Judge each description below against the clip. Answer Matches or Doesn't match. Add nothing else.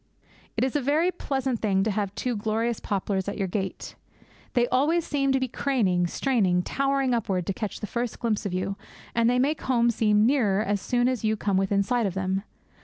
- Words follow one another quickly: Matches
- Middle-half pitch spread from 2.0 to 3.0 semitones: Doesn't match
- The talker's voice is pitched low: Doesn't match